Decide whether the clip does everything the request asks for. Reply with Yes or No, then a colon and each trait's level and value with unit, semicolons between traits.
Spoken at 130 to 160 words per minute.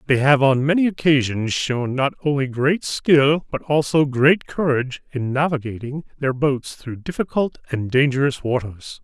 Yes: average, 155 wpm